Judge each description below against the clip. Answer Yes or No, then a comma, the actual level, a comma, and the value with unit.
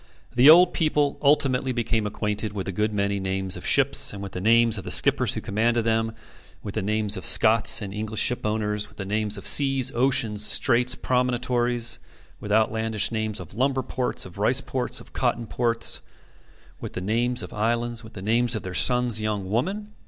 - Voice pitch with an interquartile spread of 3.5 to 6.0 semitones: No, average, 2.9 semitones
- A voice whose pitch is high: No, low, 110 Hz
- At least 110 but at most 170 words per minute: No, average, 190 wpm